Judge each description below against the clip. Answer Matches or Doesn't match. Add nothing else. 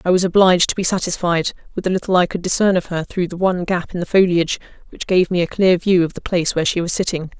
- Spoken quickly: Matches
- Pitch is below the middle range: Doesn't match